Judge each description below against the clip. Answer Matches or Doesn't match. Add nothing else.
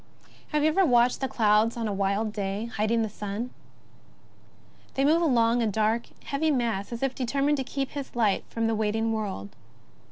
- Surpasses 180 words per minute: Matches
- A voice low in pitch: Doesn't match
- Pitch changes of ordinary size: Matches